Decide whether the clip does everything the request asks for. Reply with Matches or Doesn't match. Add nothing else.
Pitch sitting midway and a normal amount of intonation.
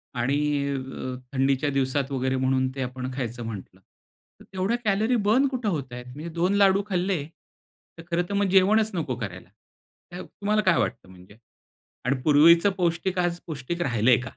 Doesn't match